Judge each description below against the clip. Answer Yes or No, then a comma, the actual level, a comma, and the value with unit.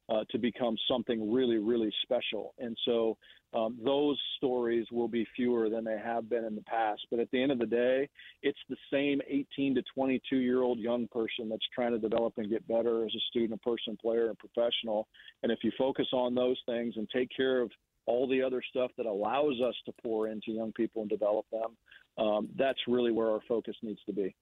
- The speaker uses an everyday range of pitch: No, narrow, 2.2 semitones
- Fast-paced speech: Yes, fast, 220 wpm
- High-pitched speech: No, low, 115 Hz